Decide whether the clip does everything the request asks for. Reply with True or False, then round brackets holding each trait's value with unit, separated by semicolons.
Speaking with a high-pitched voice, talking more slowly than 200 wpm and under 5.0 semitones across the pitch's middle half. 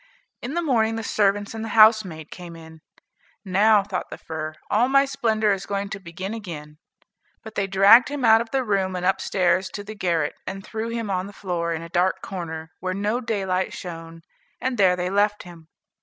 False (195 Hz; 205 wpm; 3.8 semitones)